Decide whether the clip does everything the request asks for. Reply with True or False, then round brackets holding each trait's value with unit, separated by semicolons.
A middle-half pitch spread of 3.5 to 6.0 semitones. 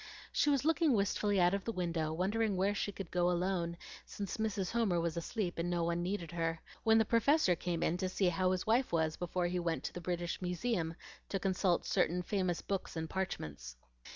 False (3.0 semitones)